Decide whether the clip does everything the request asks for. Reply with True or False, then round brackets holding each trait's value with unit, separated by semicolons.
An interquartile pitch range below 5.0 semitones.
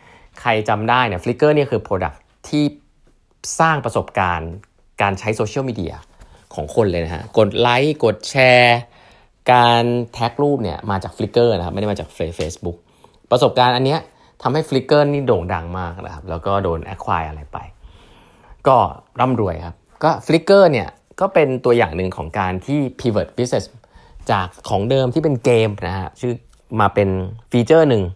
False (5.5 semitones)